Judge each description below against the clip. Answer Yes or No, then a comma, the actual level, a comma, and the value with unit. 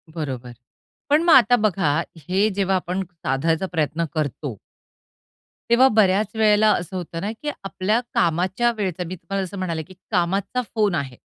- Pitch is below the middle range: No, medium, 185 Hz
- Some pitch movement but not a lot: Yes, average, 4.2 semitones